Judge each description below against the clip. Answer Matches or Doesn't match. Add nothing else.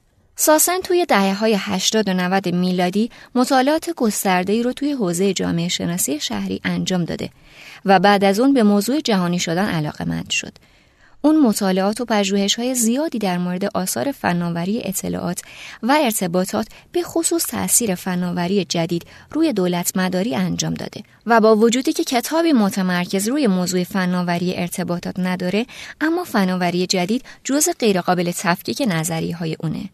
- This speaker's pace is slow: Doesn't match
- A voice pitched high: Matches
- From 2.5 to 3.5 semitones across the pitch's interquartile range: Doesn't match